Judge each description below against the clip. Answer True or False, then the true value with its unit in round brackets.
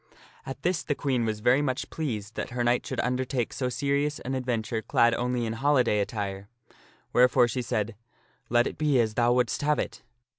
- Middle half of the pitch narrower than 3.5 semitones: True (2.7 semitones)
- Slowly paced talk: False (200 wpm)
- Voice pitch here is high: False (125 Hz)